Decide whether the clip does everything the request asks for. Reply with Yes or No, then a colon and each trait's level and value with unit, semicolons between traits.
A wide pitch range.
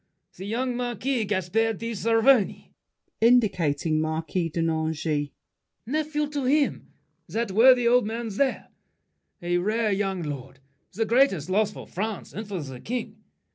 Yes: wide, 5.9 semitones